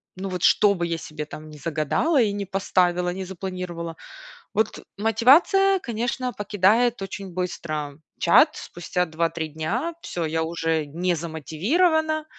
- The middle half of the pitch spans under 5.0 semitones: No, average, 5.3 semitones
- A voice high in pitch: No, medium, 180 Hz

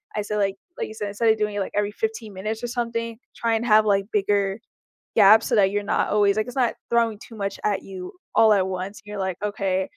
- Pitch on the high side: Yes, high, 210 Hz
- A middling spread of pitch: No, narrow, 2.0 semitones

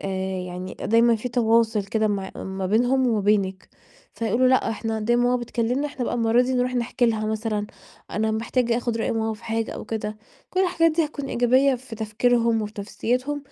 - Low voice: No, high, 230 Hz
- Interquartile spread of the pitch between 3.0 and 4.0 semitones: No, narrow, 2.4 semitones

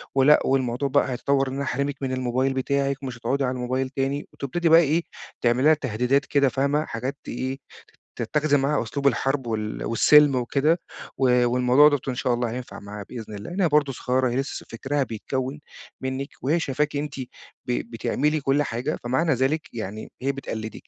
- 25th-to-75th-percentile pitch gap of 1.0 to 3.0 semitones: Yes, narrow, 2.4 semitones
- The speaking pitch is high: No, low, 135 Hz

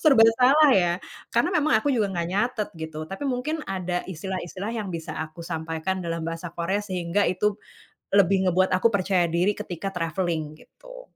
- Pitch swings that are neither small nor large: Yes, average, 3.9 semitones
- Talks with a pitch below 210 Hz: Yes, medium, 185 Hz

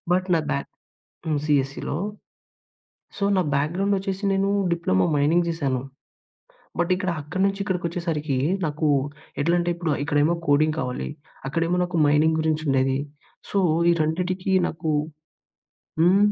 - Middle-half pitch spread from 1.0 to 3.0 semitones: No, average, 3.5 semitones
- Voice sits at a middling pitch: Yes, medium, 160 Hz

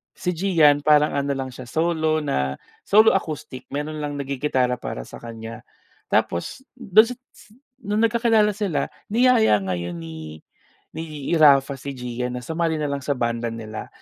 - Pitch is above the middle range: No, medium, 145 Hz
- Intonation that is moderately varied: No, wide, 5.8 semitones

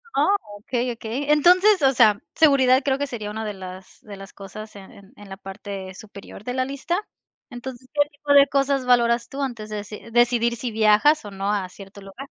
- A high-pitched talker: Yes, high, 235 Hz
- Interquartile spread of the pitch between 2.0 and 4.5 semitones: No, average, 5.0 semitones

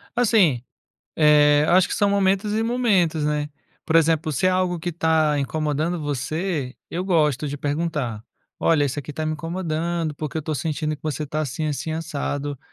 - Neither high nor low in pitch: Yes, medium, 155 Hz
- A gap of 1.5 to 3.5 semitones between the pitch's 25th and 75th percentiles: Yes, average, 2.8 semitones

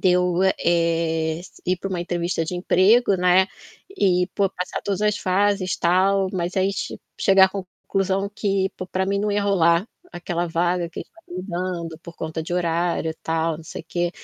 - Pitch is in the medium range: Yes, medium, 180 Hz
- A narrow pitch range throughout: Yes, narrow, 2.3 semitones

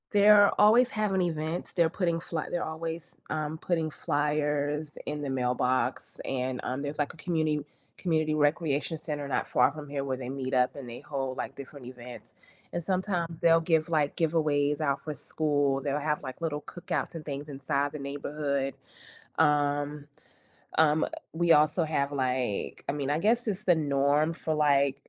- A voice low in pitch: No, medium, 150 Hz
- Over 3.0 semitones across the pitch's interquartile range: No, average, 2.7 semitones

